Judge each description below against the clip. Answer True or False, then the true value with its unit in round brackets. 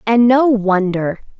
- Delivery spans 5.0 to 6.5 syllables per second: False (3.5 syllables/s)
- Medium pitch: False (215 Hz)